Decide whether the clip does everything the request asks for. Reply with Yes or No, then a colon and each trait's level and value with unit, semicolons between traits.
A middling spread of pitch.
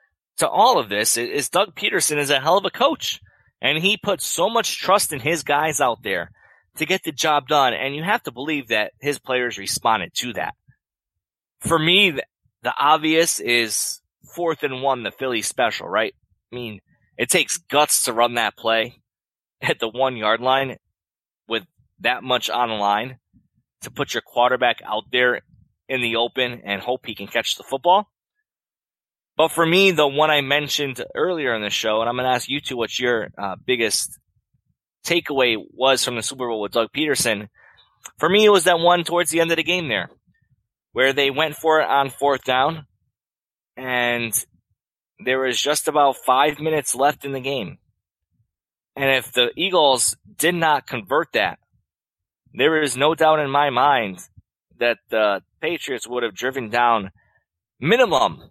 Yes: average, 4.4 semitones